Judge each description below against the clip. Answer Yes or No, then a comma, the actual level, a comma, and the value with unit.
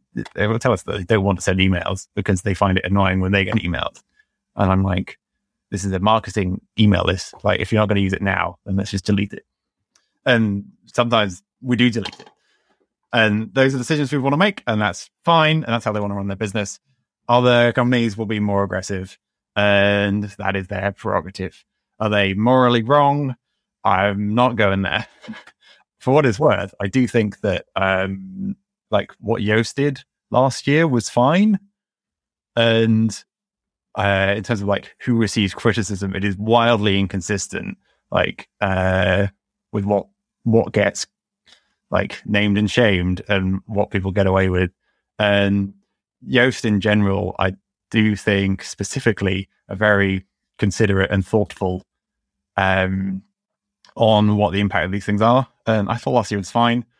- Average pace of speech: Yes, average, 175 wpm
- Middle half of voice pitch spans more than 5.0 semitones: No, average, 3.2 semitones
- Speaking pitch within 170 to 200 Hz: No, low, 105 Hz